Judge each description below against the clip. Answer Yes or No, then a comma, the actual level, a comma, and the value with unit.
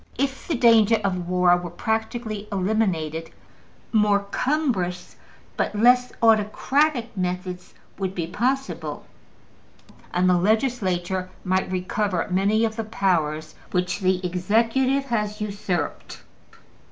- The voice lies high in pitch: Yes, high, 200 Hz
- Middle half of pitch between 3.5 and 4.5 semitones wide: Yes, average, 3.9 semitones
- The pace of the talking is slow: Yes, slow, 110 wpm